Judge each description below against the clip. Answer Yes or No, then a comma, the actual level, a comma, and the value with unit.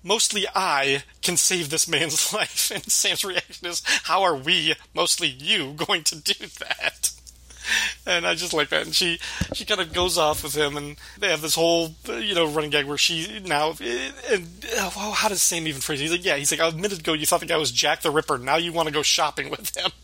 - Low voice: No, medium, 165 Hz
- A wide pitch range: No, average, 3.0 semitones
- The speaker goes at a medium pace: No, fast, 230 wpm